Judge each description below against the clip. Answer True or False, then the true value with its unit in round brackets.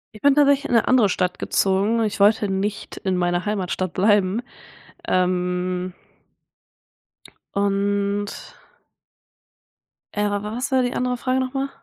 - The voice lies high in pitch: True (205 Hz)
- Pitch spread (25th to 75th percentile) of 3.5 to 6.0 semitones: True (4.4 semitones)